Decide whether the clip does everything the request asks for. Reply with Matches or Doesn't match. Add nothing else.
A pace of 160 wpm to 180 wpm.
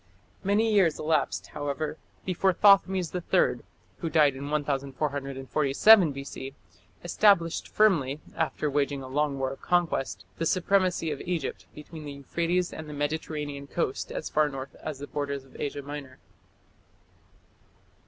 Doesn't match